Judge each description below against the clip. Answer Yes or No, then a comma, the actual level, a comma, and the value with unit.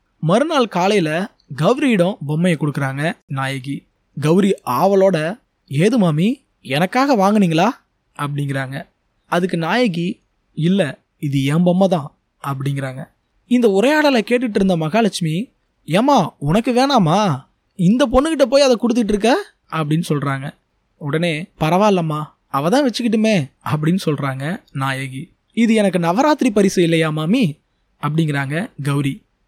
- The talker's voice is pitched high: No, medium, 175 Hz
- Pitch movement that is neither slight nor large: No, wide, 6.7 semitones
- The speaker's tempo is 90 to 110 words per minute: Yes, average, 105 wpm